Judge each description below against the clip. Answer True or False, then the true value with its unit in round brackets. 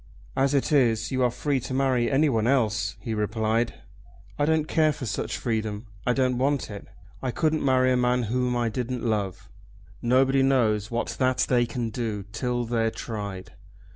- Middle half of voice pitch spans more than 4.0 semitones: False (2.9 semitones)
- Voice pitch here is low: True (125 Hz)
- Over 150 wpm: True (175 wpm)